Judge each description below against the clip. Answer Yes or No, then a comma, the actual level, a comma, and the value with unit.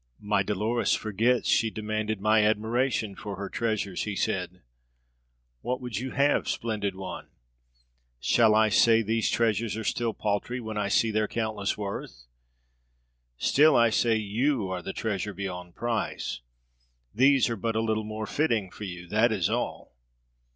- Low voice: Yes, low, 110 Hz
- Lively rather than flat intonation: No, narrow, 2.5 semitones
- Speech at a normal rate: Yes, average, 155 wpm